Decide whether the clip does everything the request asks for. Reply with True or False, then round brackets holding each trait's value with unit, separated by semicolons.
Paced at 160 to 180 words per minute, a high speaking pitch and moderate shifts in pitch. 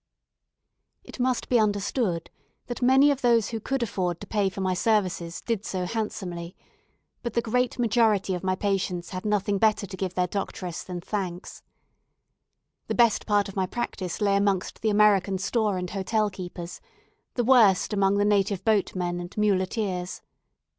True (165 wpm; 200 Hz; 3.1 semitones)